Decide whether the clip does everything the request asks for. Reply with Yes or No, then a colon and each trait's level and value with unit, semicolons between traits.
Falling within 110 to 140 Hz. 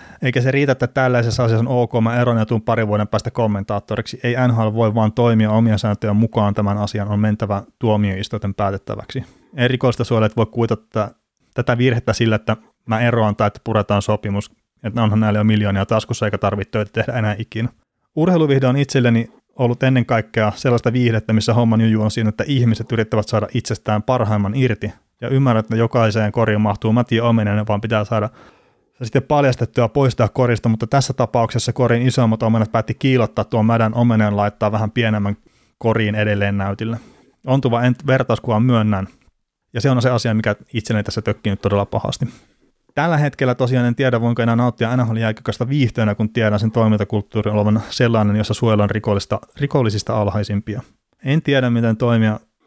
Yes: low, 115 Hz